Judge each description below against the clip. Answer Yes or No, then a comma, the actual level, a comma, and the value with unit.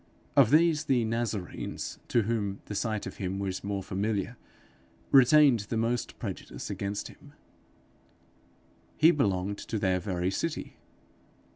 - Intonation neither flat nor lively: Yes, average, 3.8 semitones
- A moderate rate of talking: No, slow, 130 wpm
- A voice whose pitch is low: Yes, low, 110 Hz